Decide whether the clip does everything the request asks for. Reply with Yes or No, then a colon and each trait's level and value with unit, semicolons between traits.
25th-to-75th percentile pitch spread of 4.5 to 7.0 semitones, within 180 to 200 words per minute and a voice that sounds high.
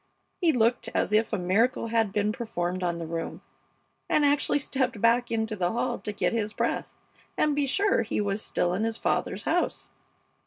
No: average, 3.9 semitones; average, 190 wpm; high, 225 Hz